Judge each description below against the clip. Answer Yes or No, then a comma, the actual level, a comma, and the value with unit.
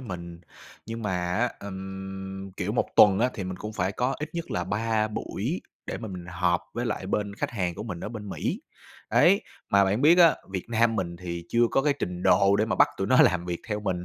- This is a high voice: No, low, 100 Hz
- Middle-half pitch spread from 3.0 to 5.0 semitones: Yes, average, 3.9 semitones